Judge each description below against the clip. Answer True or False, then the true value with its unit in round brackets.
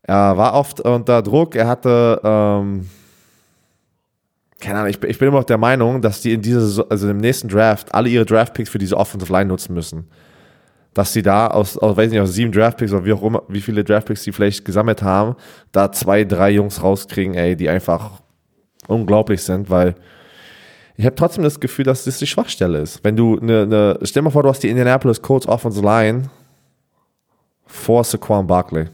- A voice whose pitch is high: False (105 Hz)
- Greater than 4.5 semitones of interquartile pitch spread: False (3.1 semitones)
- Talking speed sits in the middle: False (195 wpm)